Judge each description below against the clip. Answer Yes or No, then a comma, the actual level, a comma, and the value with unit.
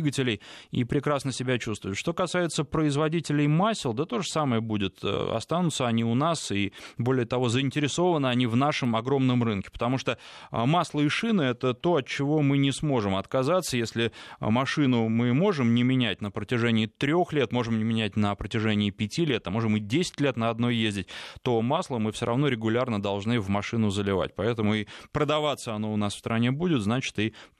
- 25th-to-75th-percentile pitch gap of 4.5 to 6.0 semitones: Yes, average, 4.9 semitones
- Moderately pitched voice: No, low, 125 Hz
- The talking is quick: Yes, fast, 185 wpm